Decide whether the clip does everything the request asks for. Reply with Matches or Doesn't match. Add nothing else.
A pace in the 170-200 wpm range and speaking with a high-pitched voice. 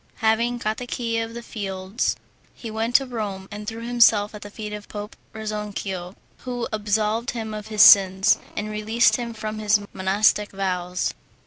Matches